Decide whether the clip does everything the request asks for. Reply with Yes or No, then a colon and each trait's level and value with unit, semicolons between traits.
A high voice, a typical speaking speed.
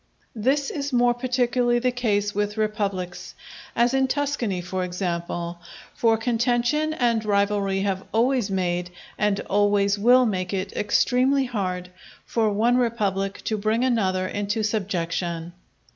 No: high, 210 Hz; slow, 130 wpm